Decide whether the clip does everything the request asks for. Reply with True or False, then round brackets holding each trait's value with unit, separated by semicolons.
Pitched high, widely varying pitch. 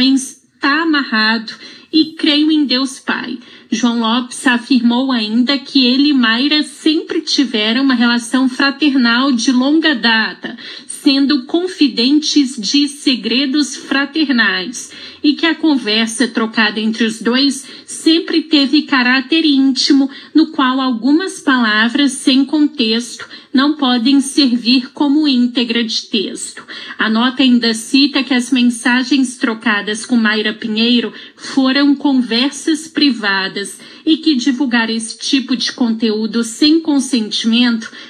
False (265 Hz; 3.5 semitones)